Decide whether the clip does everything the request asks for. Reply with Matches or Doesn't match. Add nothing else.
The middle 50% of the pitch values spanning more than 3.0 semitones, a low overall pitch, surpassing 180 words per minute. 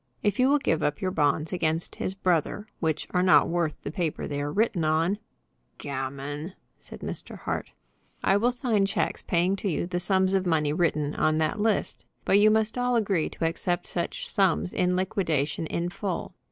Doesn't match